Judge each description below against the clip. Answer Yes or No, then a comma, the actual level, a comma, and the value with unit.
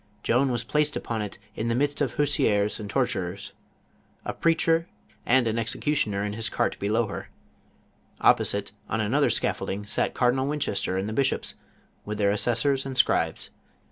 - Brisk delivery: No, average, 170 wpm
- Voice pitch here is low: Yes, low, 115 Hz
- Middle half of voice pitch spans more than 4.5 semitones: Yes, average, 4.9 semitones